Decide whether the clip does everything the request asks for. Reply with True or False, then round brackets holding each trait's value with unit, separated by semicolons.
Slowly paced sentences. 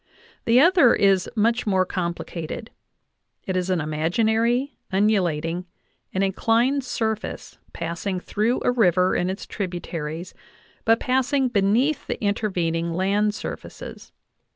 True (120 wpm)